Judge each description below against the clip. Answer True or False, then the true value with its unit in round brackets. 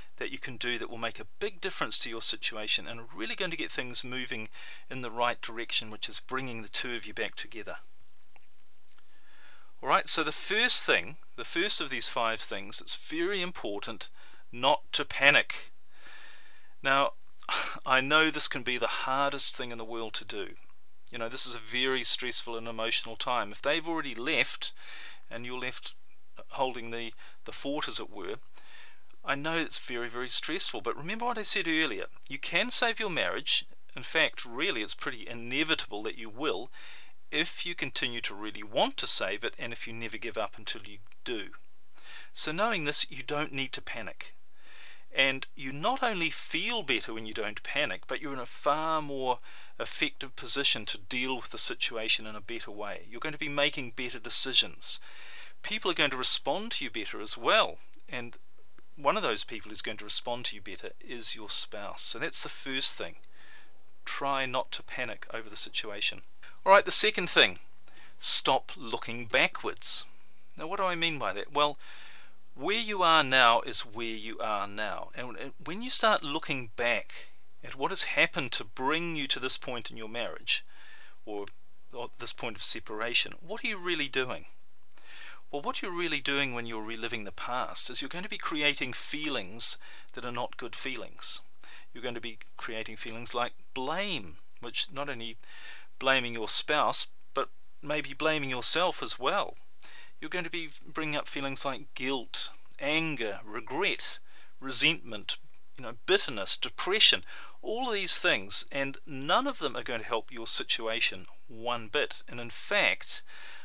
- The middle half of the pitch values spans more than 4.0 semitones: True (5.2 semitones)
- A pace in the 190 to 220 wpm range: False (180 wpm)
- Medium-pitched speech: False (130 Hz)